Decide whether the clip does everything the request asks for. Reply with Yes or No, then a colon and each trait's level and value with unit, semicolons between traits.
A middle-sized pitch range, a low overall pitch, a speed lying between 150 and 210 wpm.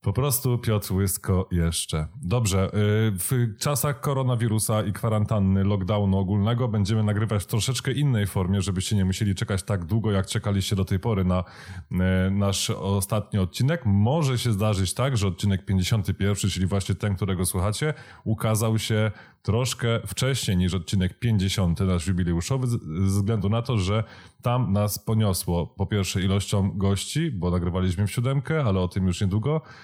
Yes: average, 3.1 semitones; low, 105 Hz; average, 155 wpm